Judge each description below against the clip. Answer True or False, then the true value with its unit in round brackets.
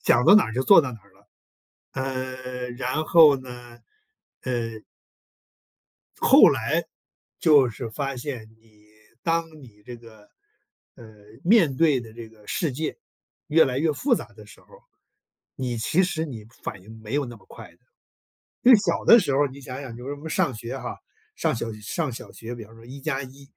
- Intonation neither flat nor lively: True (4.0 semitones)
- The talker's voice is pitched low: True (130 Hz)